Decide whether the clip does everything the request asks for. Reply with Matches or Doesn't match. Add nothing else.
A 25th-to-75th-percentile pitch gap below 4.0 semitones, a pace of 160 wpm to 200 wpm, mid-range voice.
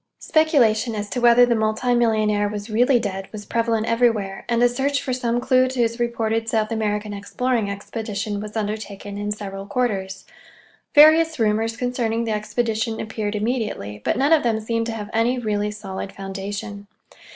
Doesn't match